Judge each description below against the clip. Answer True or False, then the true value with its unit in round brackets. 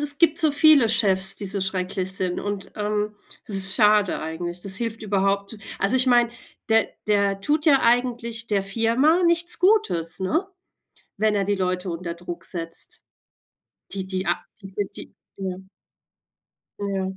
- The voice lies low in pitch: False (205 Hz)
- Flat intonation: False (3.8 semitones)